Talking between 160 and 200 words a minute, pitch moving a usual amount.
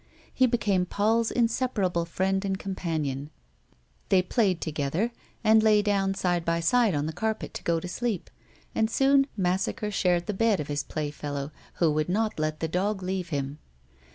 Yes: average, 175 wpm; average, 5.0 semitones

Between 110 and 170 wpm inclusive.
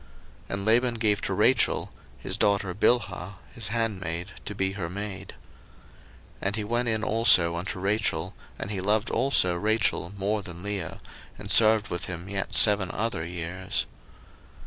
Yes: average, 160 wpm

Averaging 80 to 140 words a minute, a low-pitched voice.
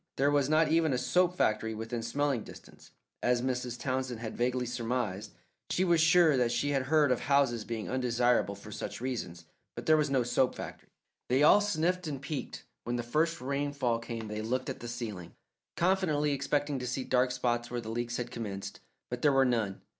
No: average, 200 wpm; low, 125 Hz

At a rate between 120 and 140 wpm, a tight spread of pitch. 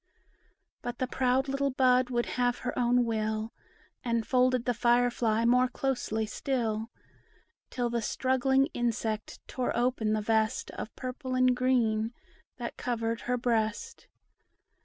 Yes: slow, 135 wpm; narrow, 2.1 semitones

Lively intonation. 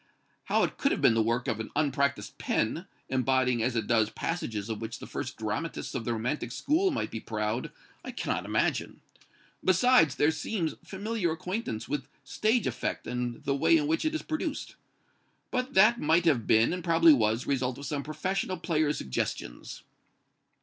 Yes: wide, 8.0 semitones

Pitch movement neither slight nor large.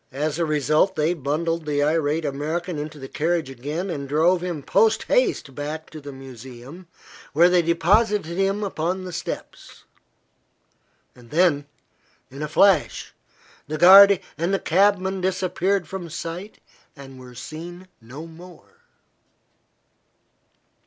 Yes: average, 4.0 semitones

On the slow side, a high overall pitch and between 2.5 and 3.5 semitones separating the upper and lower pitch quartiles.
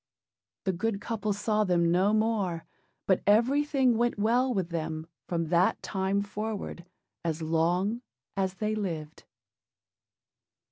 No: slow, 125 wpm; high, 200 Hz; average, 4.2 semitones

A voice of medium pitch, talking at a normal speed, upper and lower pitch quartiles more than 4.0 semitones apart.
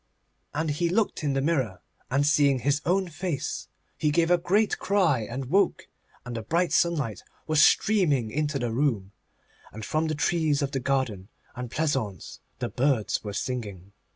Yes: medium, 145 Hz; average, 170 wpm; average, 5.1 semitones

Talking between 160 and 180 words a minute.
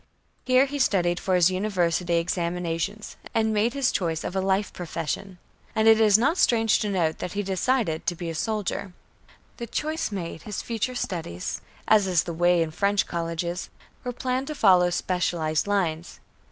Yes: average, 175 wpm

